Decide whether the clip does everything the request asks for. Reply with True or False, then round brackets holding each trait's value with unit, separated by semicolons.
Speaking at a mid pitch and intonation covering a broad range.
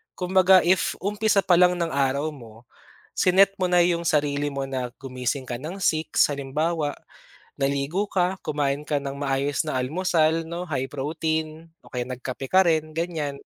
False (155 Hz; 4.2 semitones)